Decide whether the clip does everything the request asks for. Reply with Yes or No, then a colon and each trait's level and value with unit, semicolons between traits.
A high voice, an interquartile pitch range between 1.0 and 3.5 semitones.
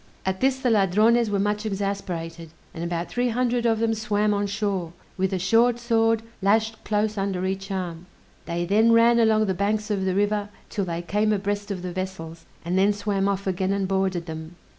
Yes: high, 200 Hz; narrow, 2.5 semitones